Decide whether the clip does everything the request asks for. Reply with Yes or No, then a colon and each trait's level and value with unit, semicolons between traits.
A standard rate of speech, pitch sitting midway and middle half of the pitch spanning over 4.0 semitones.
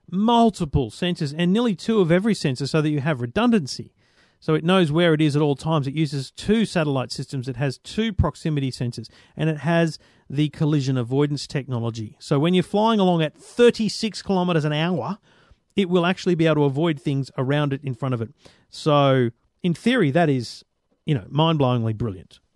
Yes: average, 190 wpm; medium, 155 Hz; average, 4.6 semitones